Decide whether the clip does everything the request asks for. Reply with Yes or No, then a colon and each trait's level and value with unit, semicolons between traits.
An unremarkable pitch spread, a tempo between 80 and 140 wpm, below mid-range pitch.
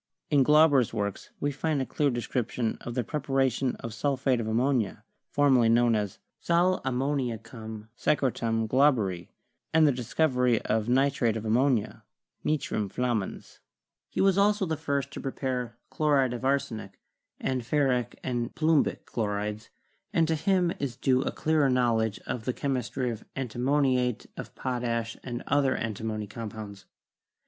No: average, 3.8 semitones; average, 150 wpm; low, 125 Hz